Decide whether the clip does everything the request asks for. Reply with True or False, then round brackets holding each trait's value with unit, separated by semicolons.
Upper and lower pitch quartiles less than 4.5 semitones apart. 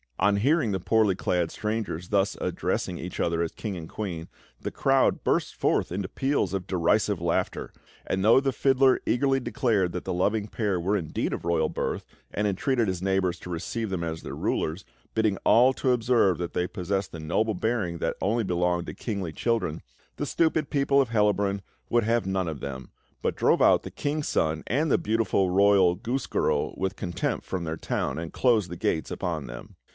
False (4.8 semitones)